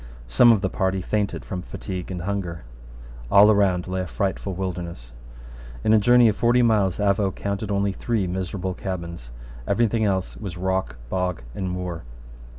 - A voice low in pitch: Yes, very low, 95 Hz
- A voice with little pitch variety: Yes, narrow, 2.1 semitones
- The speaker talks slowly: No, average, 165 wpm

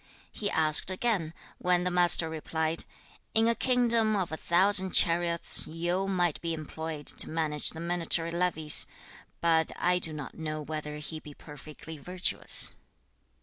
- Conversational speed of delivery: Yes, average, 150 wpm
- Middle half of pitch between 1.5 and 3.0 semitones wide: Yes, narrow, 2.4 semitones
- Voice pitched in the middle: Yes, medium, 165 Hz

